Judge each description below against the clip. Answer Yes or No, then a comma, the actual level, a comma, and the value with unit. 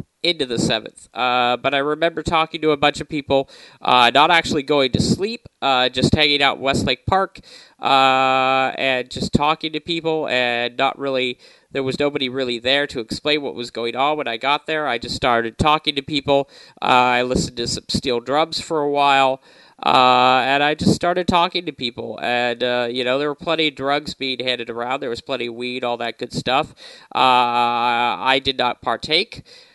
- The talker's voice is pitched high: No, low, 135 Hz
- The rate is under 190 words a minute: No, average, 200 wpm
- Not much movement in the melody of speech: No, average, 3.4 semitones